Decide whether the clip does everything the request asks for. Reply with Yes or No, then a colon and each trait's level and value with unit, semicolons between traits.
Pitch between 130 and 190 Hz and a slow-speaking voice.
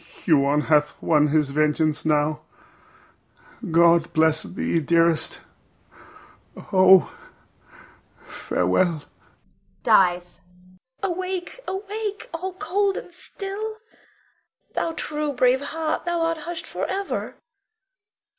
Yes: medium, 185 Hz; slow, 90 wpm